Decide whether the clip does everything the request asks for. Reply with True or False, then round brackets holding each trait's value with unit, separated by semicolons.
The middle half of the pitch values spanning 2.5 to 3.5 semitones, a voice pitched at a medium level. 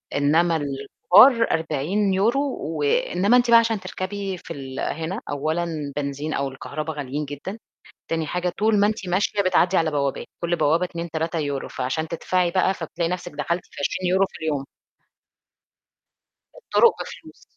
False (4.4 semitones; 170 Hz)